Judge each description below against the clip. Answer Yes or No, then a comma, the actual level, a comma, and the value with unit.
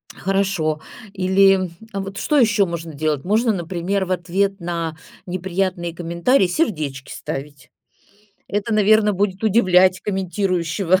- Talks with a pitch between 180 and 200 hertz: Yes, medium, 185 Hz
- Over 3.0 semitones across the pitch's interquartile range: No, narrow, 2.6 semitones